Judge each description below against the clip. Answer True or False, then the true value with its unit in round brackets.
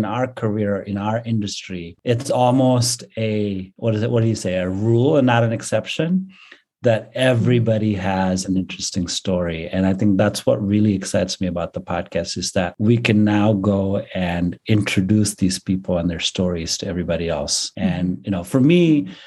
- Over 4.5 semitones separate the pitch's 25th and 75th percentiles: False (3.6 semitones)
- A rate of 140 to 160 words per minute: False (185 wpm)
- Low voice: True (105 Hz)